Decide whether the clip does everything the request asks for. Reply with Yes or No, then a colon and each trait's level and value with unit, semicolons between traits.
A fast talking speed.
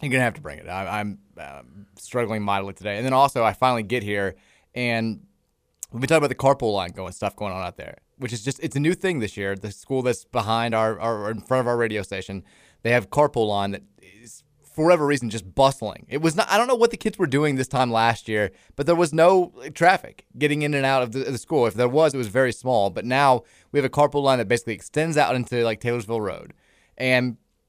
Yes: fast, 255 wpm